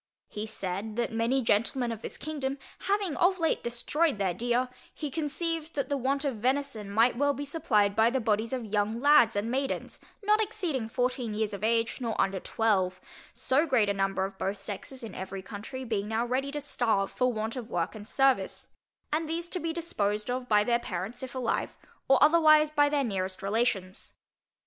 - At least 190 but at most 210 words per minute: Yes, average, 195 wpm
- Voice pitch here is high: Yes, high, 240 Hz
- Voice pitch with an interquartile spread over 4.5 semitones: Yes, average, 5.2 semitones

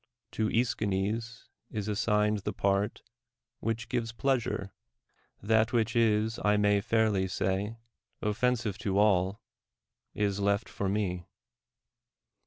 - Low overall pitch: Yes, low, 105 Hz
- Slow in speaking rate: Yes, slow, 110 wpm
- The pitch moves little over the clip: Yes, narrow, 2.1 semitones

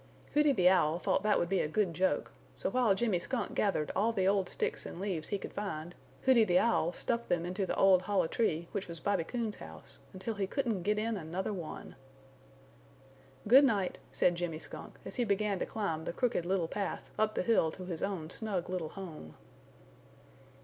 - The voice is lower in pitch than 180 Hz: No, high, 190 Hz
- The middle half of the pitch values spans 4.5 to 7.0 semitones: No, average, 3.7 semitones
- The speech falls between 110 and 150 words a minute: No, average, 200 wpm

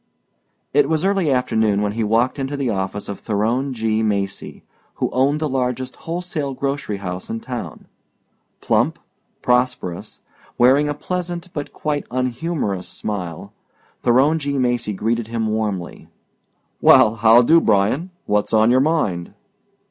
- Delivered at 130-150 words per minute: Yes, average, 140 wpm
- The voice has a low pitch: Yes, low, 125 Hz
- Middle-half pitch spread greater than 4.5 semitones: Yes, average, 5.1 semitones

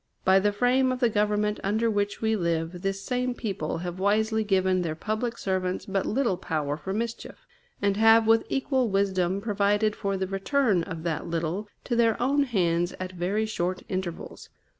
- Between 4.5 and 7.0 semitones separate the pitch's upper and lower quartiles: No, average, 3.4 semitones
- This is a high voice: Yes, high, 200 Hz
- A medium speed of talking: Yes, average, 180 wpm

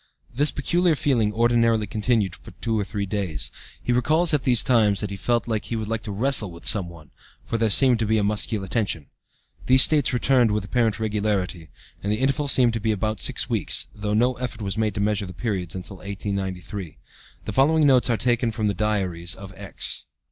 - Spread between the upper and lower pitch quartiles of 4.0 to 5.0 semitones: No, average, 3.4 semitones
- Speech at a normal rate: No, fast, 210 wpm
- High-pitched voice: No, low, 110 Hz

